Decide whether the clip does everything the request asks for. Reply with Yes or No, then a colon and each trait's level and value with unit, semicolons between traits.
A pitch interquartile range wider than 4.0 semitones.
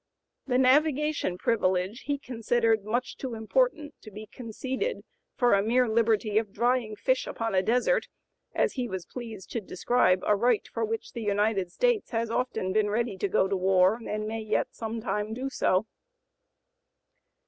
No: average, 3.3 semitones